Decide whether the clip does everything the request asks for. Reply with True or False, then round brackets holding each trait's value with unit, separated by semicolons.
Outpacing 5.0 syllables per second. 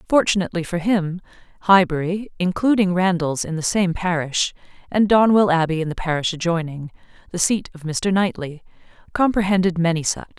True (5.5 syllables/s)